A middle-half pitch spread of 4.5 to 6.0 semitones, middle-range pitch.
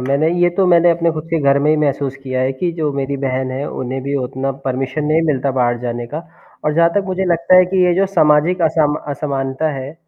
No: average, 4.0 semitones; medium, 150 Hz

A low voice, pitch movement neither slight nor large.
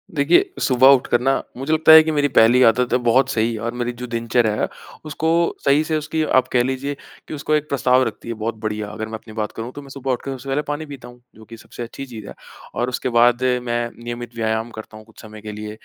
Yes: low, 120 Hz; average, 3.5 semitones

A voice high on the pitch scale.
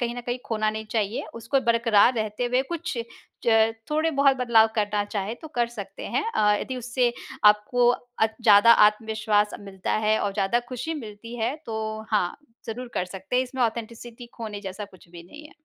Yes: high, 225 Hz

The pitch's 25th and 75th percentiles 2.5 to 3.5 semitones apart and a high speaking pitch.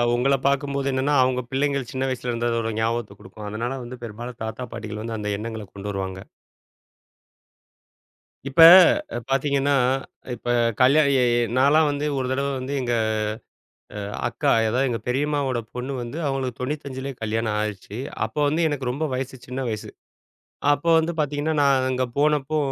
No: average, 3.2 semitones; low, 130 Hz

